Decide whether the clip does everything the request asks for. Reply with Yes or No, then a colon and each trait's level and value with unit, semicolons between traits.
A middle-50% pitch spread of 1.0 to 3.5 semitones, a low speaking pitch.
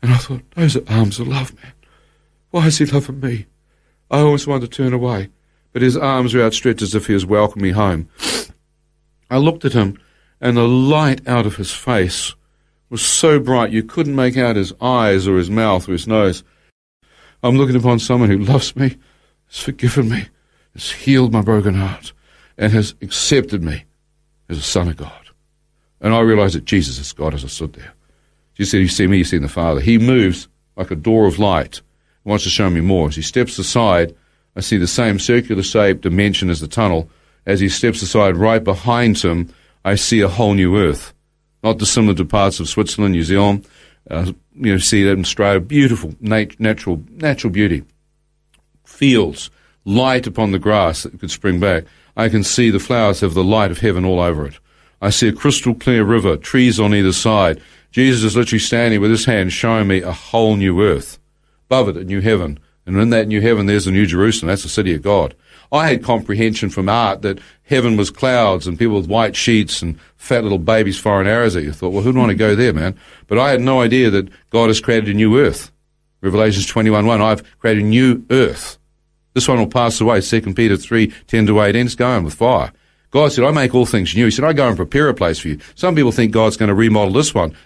No: average, 4.3 semitones; low, 110 Hz